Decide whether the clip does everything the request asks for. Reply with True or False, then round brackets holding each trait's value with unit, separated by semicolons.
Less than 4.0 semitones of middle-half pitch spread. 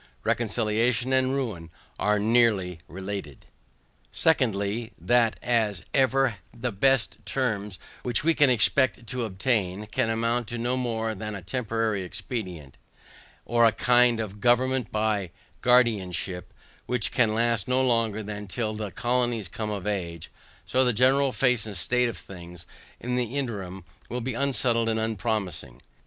True (3.3 semitones)